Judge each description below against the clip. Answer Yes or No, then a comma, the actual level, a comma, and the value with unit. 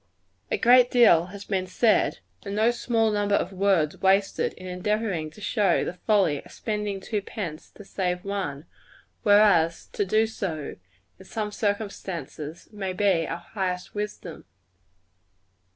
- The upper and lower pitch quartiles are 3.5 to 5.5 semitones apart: No, average, 2.8 semitones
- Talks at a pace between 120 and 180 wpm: Yes, average, 145 wpm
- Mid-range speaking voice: No, high, 195 Hz